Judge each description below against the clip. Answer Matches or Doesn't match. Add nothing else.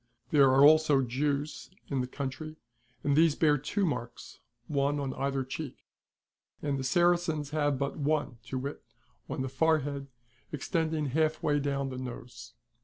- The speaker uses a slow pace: Doesn't match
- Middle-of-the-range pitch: Matches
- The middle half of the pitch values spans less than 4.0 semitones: Matches